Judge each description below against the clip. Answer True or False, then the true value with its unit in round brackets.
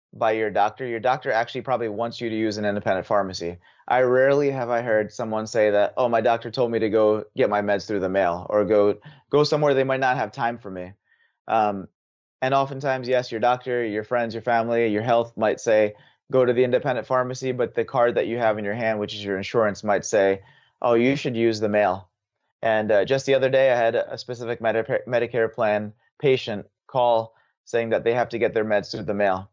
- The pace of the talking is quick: True (225 wpm)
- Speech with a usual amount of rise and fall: True (3.2 semitones)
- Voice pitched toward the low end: True (115 Hz)